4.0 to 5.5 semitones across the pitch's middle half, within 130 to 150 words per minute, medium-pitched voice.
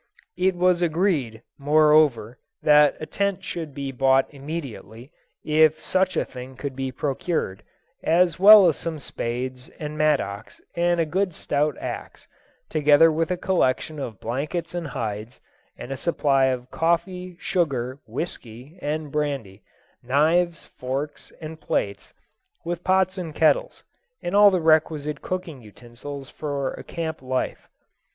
Yes: average, 4.5 semitones; average, 140 wpm; medium, 150 Hz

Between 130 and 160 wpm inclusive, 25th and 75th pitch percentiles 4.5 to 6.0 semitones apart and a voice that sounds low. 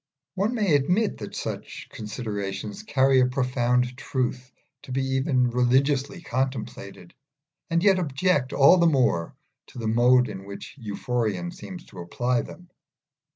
Yes: average, 140 wpm; average, 5.0 semitones; low, 130 Hz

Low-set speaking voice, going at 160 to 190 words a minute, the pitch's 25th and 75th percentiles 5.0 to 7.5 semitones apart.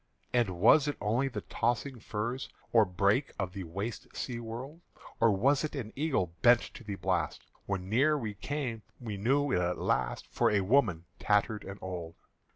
Yes: low, 110 Hz; average, 180 wpm; average, 5.3 semitones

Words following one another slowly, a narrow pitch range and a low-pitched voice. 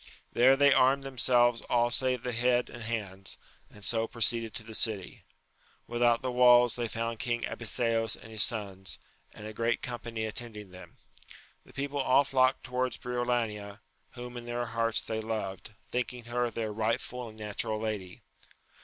No: average, 165 wpm; narrow, 2.1 semitones; low, 120 Hz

